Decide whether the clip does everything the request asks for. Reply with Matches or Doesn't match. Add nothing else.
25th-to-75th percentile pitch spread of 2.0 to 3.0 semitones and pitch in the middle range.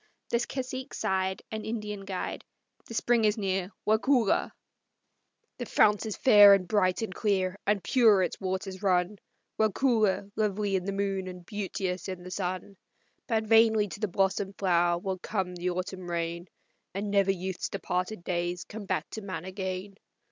Doesn't match